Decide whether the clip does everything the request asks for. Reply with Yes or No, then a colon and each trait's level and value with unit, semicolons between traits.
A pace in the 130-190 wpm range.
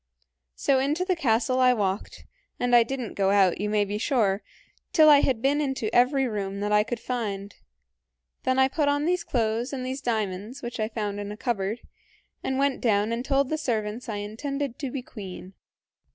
No: average, 200 wpm